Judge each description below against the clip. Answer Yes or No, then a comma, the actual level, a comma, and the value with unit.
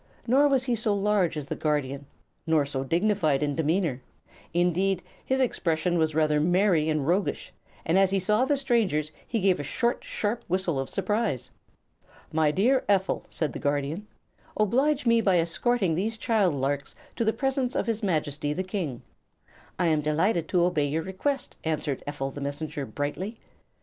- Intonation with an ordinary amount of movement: No, wide, 6.0 semitones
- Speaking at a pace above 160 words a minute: Yes, average, 170 wpm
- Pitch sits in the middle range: Yes, medium, 175 Hz